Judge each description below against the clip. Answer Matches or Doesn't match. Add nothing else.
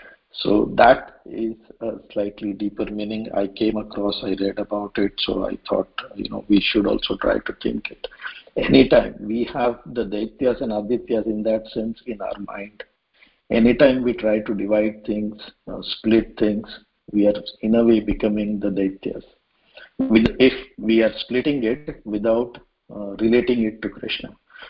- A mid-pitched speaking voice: Doesn't match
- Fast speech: Doesn't match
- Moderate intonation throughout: Doesn't match